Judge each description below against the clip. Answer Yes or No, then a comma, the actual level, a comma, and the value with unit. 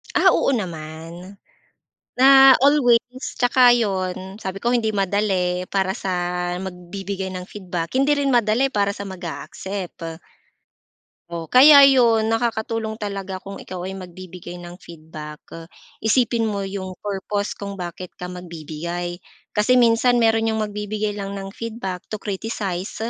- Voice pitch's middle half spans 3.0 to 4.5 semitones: Yes, average, 3.9 semitones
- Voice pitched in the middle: No, high, 200 Hz